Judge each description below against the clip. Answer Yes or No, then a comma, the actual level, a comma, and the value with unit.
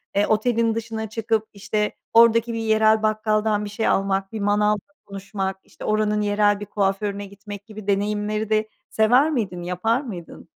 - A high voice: Yes, high, 210 Hz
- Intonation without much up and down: Yes, narrow, 1.5 semitones